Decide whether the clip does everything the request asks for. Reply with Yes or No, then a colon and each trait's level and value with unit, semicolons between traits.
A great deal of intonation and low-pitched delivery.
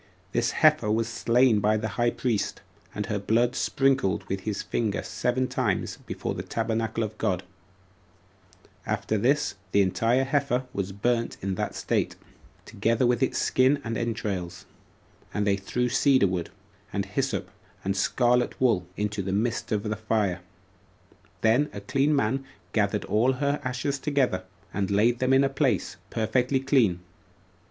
No: average, 4.0 semitones; low, 115 Hz